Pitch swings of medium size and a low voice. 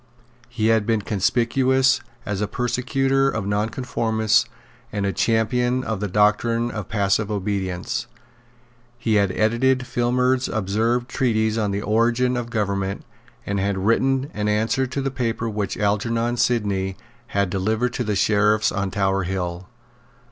Yes: average, 3.2 semitones; low, 110 Hz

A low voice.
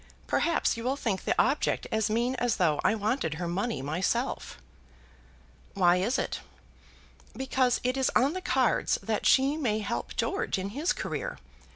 No: high, 230 Hz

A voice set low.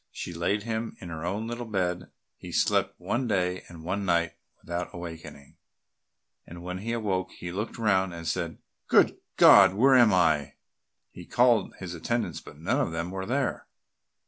Yes: very low, 95 Hz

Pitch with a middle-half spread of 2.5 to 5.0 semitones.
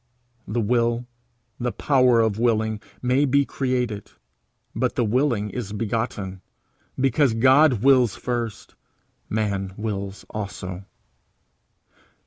Yes: average, 3.3 semitones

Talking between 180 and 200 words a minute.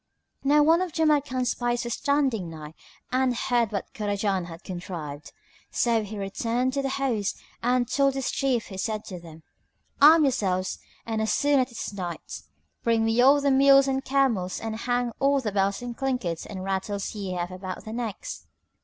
Yes: average, 185 wpm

